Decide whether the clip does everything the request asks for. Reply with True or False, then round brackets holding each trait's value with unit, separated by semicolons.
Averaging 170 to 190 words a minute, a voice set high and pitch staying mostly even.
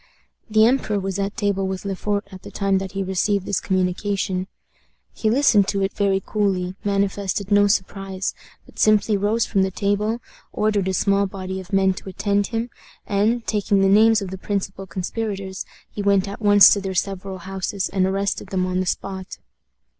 True (185 wpm; 195 Hz; 1.4 semitones)